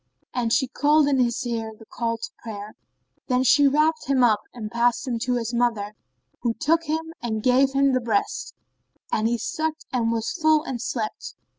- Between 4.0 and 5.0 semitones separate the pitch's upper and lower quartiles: No, average, 3.5 semitones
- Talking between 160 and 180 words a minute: No, average, 190 wpm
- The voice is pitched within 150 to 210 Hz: No, high, 245 Hz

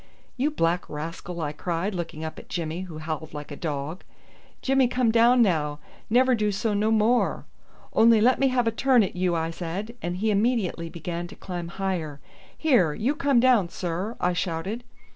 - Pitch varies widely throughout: Yes, wide, 5.9 semitones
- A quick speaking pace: No, average, 185 wpm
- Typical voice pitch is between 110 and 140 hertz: No, medium, 185 Hz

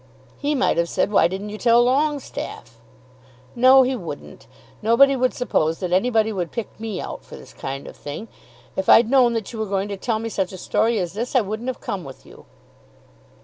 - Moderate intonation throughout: Yes, average, 4.6 semitones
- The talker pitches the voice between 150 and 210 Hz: No, high, 220 Hz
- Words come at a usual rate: No, fast, 210 wpm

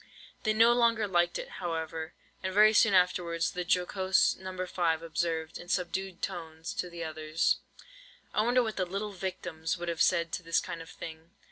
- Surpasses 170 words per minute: Yes, average, 180 wpm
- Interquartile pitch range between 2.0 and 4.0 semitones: Yes, narrow, 2.5 semitones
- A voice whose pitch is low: No, medium, 175 Hz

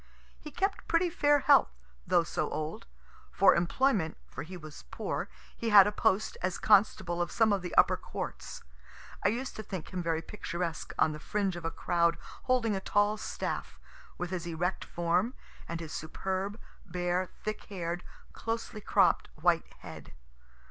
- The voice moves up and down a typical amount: Yes, average, 4.0 semitones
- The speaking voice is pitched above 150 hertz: Yes, medium, 185 Hz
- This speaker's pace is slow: No, average, 165 wpm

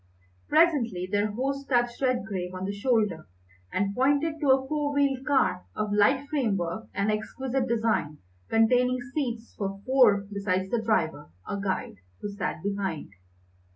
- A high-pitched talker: Yes, high, 225 Hz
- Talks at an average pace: Yes, average, 145 wpm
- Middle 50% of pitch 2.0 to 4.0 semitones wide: No, average, 5.0 semitones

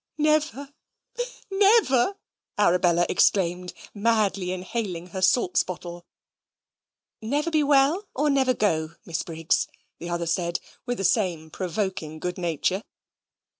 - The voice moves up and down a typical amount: No, wide, 7.6 semitones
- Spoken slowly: Yes, slow, 115 wpm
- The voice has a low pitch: No, high, 190 Hz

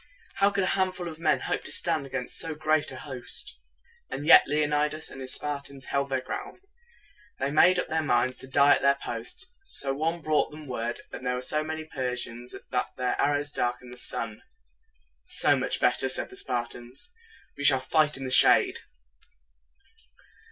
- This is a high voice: No, medium, 145 Hz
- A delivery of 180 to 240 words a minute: Yes, average, 200 wpm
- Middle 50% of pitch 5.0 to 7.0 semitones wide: No, average, 3.6 semitones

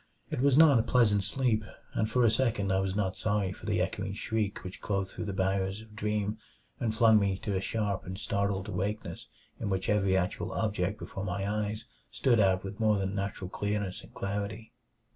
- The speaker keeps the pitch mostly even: Yes, narrow, 2.1 semitones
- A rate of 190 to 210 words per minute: Yes, average, 200 wpm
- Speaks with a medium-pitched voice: No, low, 100 Hz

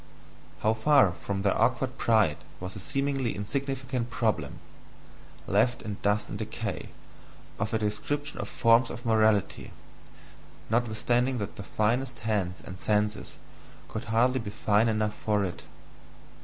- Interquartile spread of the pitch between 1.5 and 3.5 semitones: Yes, average, 3.2 semitones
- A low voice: Yes, low, 110 Hz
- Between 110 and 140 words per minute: Yes, slow, 135 wpm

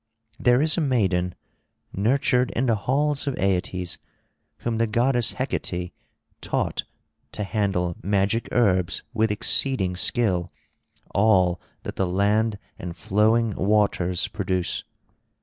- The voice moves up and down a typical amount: Yes, average, 4.5 semitones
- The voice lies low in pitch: Yes, low, 105 Hz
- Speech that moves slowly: Yes, slow, 115 wpm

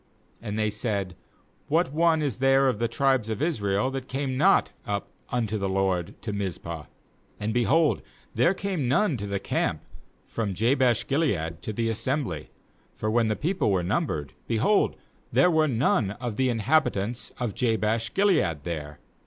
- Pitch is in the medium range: No, low, 115 Hz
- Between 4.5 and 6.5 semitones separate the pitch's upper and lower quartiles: Yes, average, 5.2 semitones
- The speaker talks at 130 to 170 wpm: Yes, average, 165 wpm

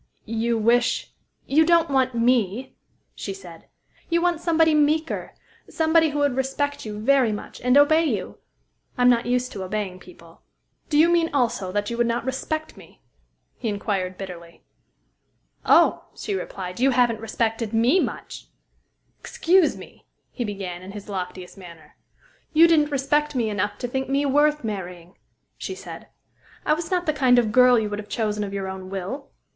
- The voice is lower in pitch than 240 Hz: No, high, 245 Hz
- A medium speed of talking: Yes, average, 170 wpm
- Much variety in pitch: Yes, wide, 6.3 semitones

